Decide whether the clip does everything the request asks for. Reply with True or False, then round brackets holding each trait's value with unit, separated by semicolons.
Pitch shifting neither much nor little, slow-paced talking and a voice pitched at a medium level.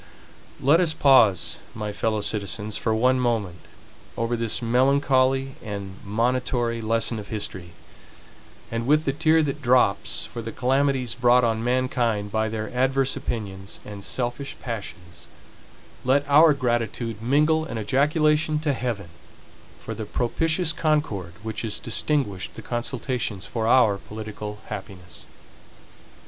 False (4.0 semitones; 130 wpm; 120 Hz)